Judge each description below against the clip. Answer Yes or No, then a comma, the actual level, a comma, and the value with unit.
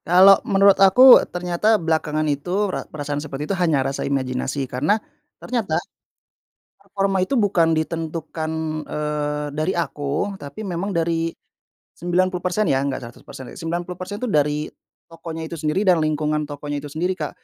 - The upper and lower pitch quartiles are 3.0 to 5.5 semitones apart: Yes, average, 3.5 semitones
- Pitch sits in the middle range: Yes, medium, 160 Hz